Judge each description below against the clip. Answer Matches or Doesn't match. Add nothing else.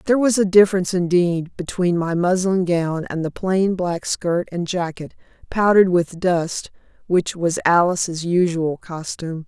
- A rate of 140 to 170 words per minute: Matches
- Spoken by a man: Doesn't match